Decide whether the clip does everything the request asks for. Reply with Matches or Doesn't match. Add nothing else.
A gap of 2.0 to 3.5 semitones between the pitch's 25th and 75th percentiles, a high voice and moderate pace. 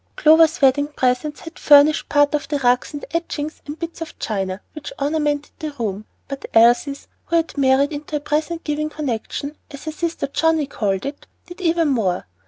Matches